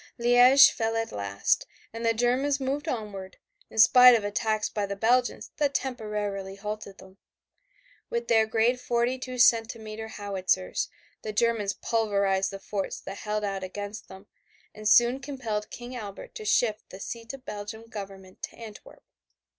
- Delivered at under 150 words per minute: No, average, 155 wpm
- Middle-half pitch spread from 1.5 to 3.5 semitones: Yes, average, 3.1 semitones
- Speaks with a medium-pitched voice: No, high, 220 Hz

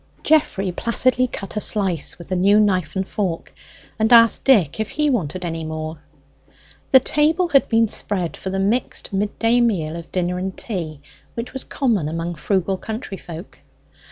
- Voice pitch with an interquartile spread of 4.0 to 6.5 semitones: Yes, average, 5.1 semitones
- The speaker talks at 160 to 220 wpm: Yes, average, 165 wpm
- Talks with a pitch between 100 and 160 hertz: No, high, 195 Hz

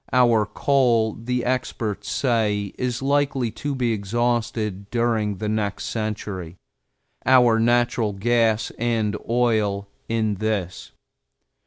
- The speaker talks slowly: Yes, slow, 110 wpm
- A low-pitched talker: Yes, low, 115 Hz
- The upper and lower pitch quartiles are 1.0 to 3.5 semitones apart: Yes, narrow, 2.4 semitones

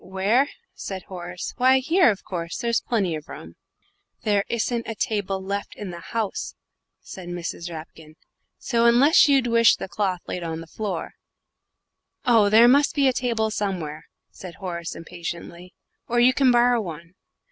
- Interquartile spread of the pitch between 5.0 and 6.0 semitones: Yes, wide, 5.4 semitones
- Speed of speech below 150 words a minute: No, average, 165 wpm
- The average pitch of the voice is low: No, high, 200 Hz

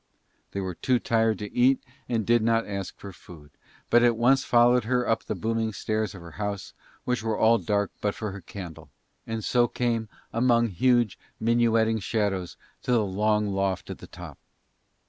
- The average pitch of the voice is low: Yes, low, 110 Hz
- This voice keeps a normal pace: Yes, average, 185 wpm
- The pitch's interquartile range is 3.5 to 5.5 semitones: No, average, 2.9 semitones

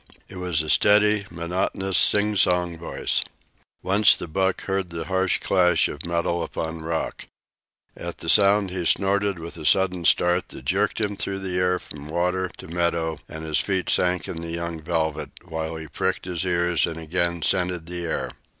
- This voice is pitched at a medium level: No, very low, 90 Hz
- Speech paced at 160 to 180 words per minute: Yes, average, 175 wpm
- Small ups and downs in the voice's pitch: Yes, narrow, 2.3 semitones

